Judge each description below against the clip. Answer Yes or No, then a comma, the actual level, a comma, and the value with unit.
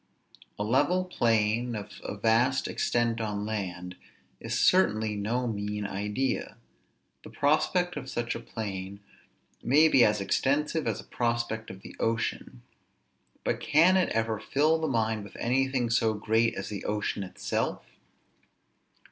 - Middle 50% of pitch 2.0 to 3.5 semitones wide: No, average, 4.1 semitones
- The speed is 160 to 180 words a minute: No, average, 140 wpm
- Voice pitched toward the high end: No, low, 115 Hz